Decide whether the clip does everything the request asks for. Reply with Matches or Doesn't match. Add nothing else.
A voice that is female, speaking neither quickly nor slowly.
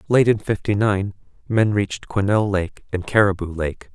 Doesn't match